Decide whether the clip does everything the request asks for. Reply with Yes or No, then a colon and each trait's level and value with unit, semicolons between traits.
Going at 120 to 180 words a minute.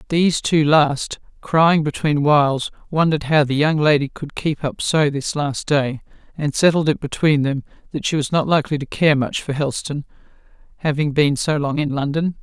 No: average, 190 wpm